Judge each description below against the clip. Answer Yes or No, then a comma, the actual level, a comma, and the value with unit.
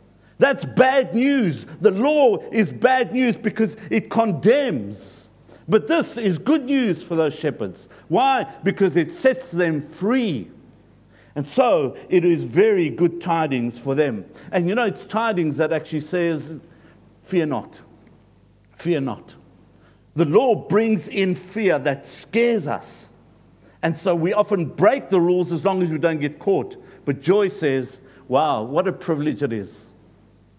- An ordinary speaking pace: Yes, average, 150 wpm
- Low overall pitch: No, medium, 175 Hz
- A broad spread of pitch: Yes, wide, 7.0 semitones